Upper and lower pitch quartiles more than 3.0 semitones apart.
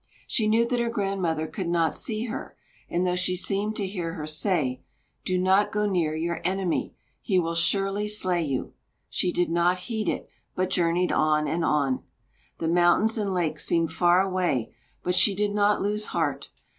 Yes: average, 3.4 semitones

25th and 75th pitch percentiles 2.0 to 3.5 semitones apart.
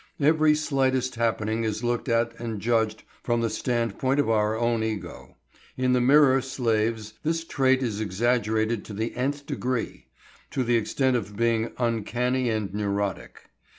Yes: average, 2.9 semitones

